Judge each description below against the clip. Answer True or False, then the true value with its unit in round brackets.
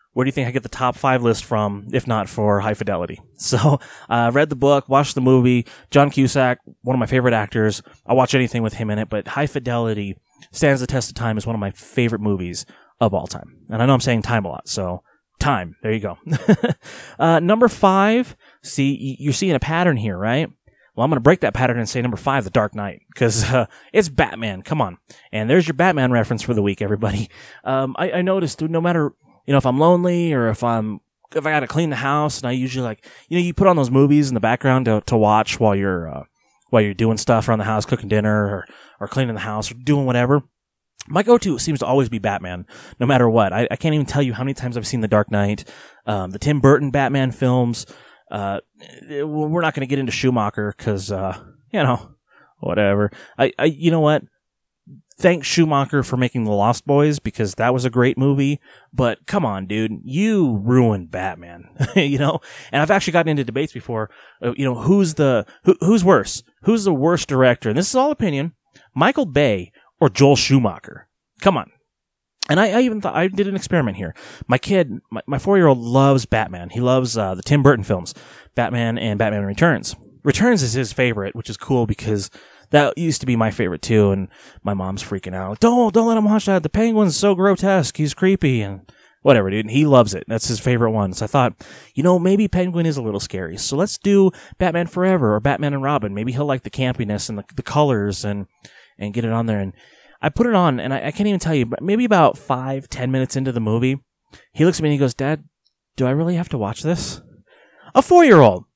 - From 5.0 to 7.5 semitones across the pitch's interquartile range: True (5.4 semitones)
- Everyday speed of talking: False (230 wpm)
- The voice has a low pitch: True (130 Hz)